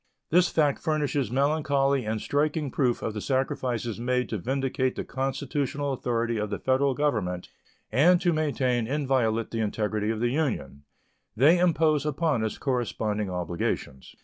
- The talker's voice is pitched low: Yes, low, 130 Hz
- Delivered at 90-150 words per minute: Yes, average, 145 wpm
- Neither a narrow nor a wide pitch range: Yes, average, 4.5 semitones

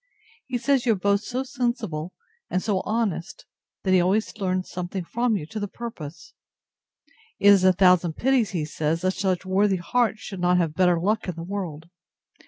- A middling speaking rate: Yes, average, 190 wpm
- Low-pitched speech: No, high, 190 Hz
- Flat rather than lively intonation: No, average, 3.7 semitones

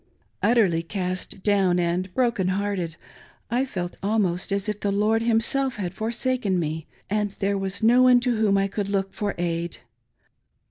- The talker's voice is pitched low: No, high, 200 Hz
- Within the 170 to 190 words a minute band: No, average, 160 wpm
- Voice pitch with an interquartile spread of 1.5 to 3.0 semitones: No, average, 3.4 semitones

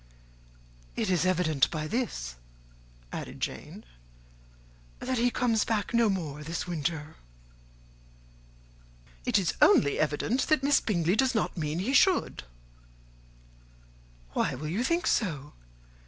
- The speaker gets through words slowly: Yes, slow, 120 wpm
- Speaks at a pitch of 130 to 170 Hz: No, medium, 185 Hz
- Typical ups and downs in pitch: No, wide, 7.9 semitones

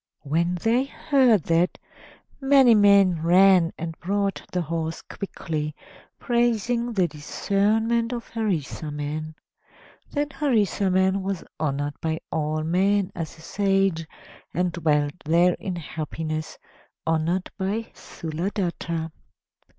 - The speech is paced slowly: Yes, slow, 105 wpm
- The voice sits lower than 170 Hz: No, medium, 180 Hz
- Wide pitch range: No, average, 4.2 semitones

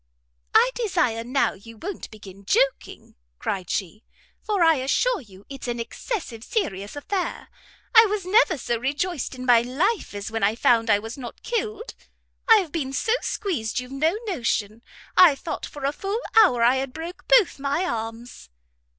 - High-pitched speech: Yes, very high, 275 Hz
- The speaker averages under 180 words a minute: Yes, average, 165 wpm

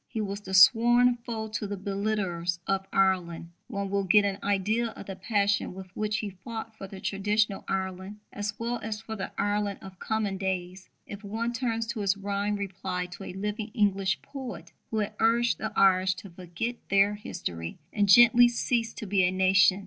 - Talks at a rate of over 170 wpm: Yes, average, 190 wpm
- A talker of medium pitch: No, high, 200 Hz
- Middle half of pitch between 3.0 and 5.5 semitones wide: No, narrow, 2.6 semitones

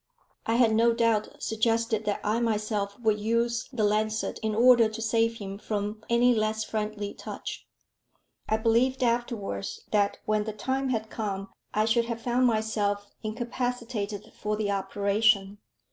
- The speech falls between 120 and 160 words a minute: Yes, average, 150 wpm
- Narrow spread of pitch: Yes, narrow, 1.9 semitones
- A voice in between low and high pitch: No, high, 220 Hz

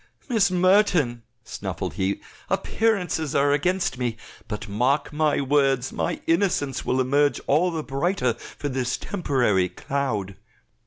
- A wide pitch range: Yes, wide, 5.7 semitones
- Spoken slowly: Yes, slow, 125 wpm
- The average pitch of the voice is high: No, medium, 140 Hz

